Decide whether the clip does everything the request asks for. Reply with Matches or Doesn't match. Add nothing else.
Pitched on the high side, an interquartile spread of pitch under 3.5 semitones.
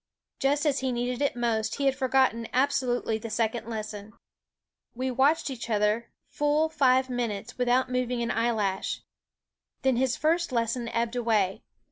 Matches